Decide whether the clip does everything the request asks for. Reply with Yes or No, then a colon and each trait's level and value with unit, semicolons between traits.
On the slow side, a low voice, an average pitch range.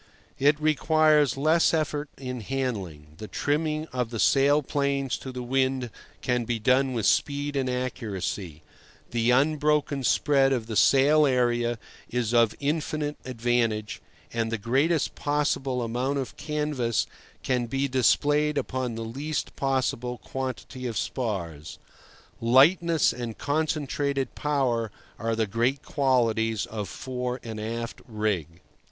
Yes: slow, 130 wpm; low, 130 Hz; average, 3.7 semitones